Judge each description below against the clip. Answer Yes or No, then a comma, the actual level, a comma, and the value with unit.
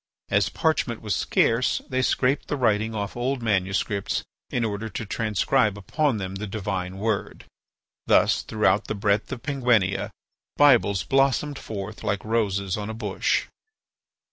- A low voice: Yes, low, 110 Hz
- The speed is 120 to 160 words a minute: Yes, average, 140 wpm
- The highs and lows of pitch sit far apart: No, average, 3.7 semitones